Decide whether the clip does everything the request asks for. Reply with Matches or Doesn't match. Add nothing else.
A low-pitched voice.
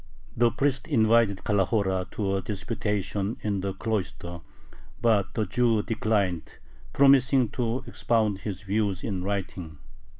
Matches